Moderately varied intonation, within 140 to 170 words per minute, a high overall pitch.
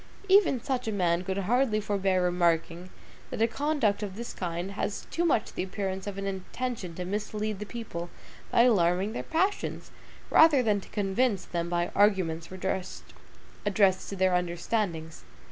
Yes: average, 3.7 semitones; average, 160 wpm; high, 195 Hz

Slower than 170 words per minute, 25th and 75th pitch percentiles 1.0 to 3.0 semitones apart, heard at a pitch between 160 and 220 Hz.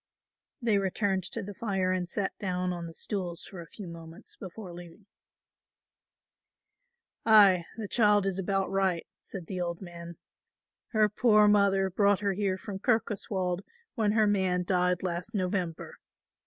Yes: average, 150 wpm; narrow, 2.4 semitones; high, 190 Hz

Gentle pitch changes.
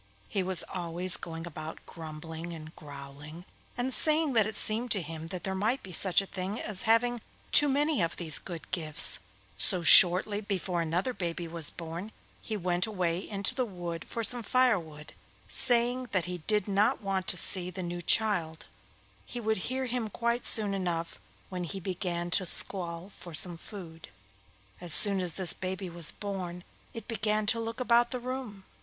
No: average, 4.4 semitones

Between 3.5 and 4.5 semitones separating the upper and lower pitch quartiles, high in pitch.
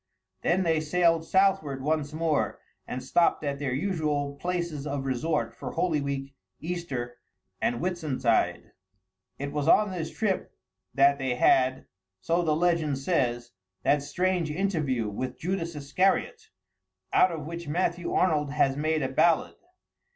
No: average, 3.8 semitones; medium, 155 Hz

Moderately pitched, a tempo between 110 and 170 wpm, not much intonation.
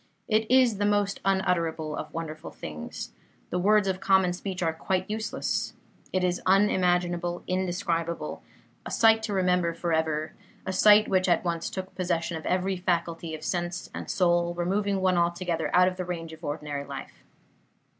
Yes: medium, 180 Hz; average, 165 wpm; narrow, 2.3 semitones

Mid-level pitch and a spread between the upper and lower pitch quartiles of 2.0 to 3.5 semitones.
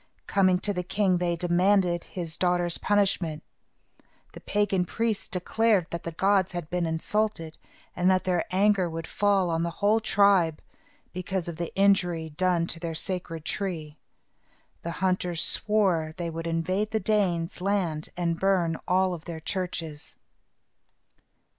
Yes: medium, 180 Hz; average, 2.7 semitones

